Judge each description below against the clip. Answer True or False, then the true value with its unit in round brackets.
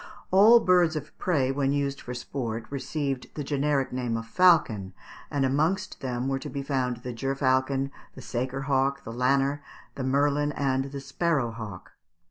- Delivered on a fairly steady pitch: True (2.2 semitones)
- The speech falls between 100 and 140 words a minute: False (165 wpm)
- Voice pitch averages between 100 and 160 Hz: True (135 Hz)